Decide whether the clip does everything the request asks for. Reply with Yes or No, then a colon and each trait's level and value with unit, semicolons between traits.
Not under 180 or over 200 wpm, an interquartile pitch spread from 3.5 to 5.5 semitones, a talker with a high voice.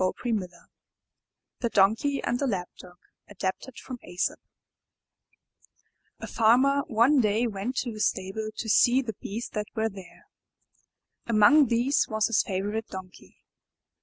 No: average, 145 wpm; average, 3.9 semitones; high, 220 Hz